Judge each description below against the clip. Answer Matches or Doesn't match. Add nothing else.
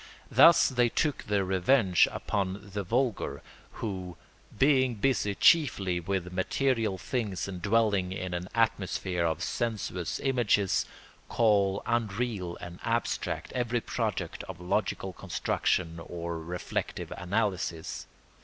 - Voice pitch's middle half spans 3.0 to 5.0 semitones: Matches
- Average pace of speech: Doesn't match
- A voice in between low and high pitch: Doesn't match